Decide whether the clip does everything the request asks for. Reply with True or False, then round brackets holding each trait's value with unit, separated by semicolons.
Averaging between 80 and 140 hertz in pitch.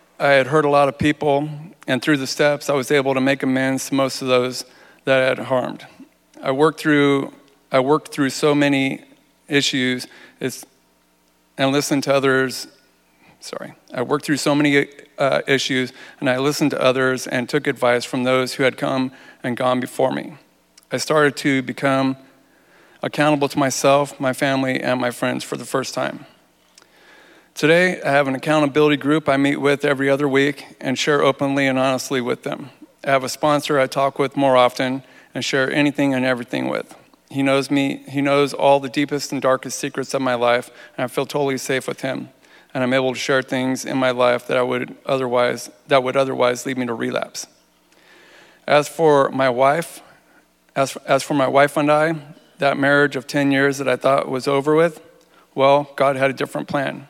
True (135 Hz)